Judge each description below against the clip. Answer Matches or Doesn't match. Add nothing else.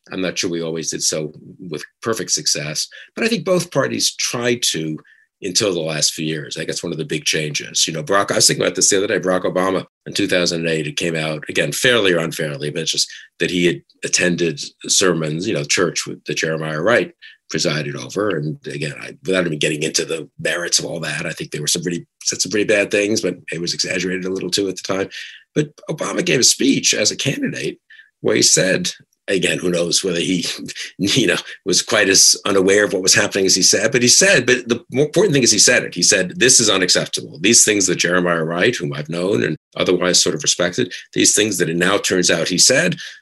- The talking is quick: Matches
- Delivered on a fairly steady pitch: Doesn't match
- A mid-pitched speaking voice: Doesn't match